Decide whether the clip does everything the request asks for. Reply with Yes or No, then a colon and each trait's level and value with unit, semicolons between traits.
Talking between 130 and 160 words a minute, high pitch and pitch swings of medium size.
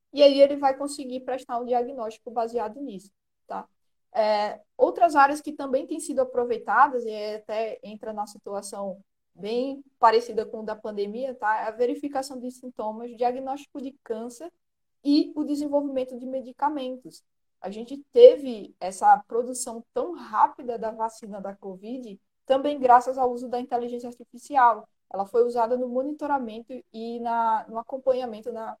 Yes: average, 150 wpm; high, 245 Hz; average, 3.4 semitones